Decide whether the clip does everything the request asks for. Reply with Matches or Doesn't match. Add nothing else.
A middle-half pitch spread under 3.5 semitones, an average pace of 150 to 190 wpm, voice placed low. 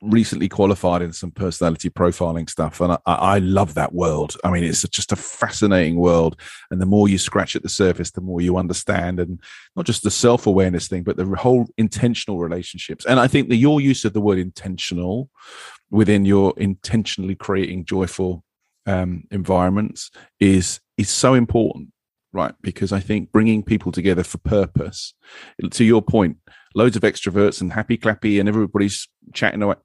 Matches